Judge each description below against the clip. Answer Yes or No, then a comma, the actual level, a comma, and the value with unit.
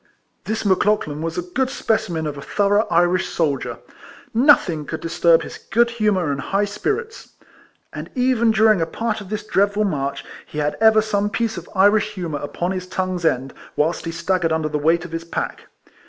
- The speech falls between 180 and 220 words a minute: Yes, average, 190 wpm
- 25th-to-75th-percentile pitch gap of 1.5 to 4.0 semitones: No, average, 4.7 semitones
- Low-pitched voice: No, medium, 185 Hz